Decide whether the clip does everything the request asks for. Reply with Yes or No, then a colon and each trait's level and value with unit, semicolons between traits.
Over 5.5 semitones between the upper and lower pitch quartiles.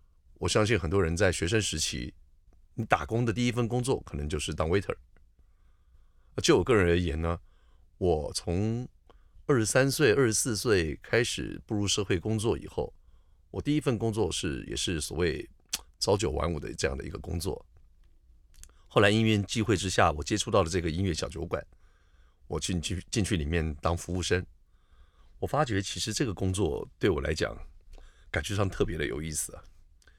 No: average, 5.1 semitones